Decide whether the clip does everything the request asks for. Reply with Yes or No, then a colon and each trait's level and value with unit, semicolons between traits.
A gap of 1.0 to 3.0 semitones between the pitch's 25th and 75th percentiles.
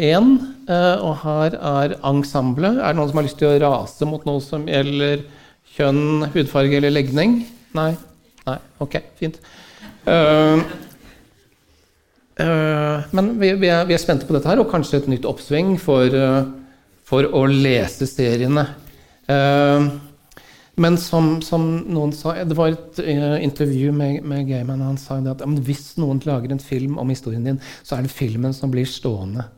Yes: average, 2.7 semitones